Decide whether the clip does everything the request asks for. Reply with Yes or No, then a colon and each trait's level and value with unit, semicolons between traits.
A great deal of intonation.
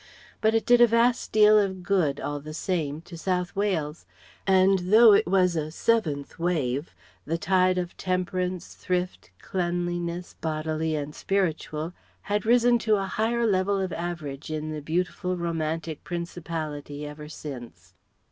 No: average, 3.8 semitones